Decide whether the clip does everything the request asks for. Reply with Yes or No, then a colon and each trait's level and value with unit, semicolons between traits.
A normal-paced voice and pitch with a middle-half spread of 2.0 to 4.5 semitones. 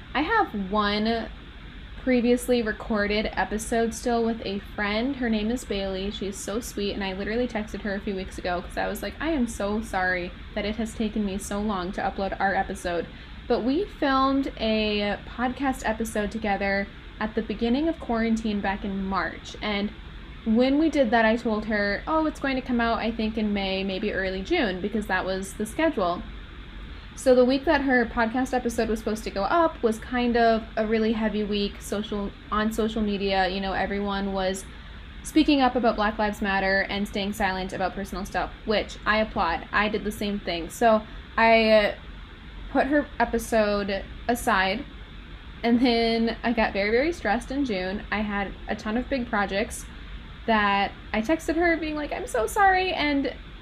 Yes: average, 185 wpm; average, 3.1 semitones